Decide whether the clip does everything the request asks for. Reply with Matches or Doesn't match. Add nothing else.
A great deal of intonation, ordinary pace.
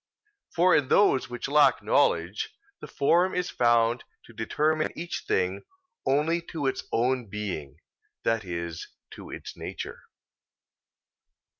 Doesn't match